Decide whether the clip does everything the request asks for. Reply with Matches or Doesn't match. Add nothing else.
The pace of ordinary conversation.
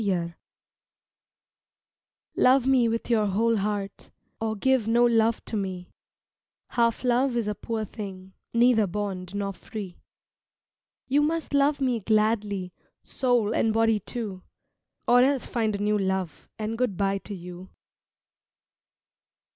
Doesn't match